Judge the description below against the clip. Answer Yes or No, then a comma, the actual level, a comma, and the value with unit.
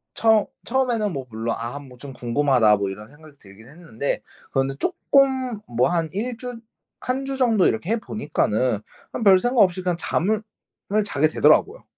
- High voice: No, medium, 165 Hz